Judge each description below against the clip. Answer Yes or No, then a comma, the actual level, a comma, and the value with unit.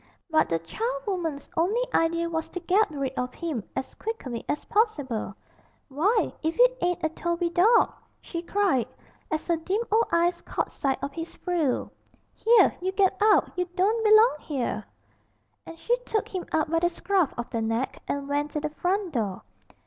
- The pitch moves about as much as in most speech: No, wide, 5.8 semitones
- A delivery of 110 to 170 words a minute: No, average, 180 wpm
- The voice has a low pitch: No, very high, 340 Hz